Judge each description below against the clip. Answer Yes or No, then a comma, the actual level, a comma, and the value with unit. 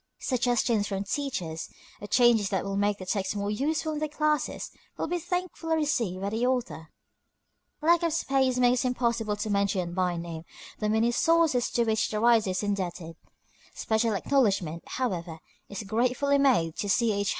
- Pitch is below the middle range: No, high, 225 Hz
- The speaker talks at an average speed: Yes, average, 170 wpm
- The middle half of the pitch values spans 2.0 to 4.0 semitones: No, average, 4.9 semitones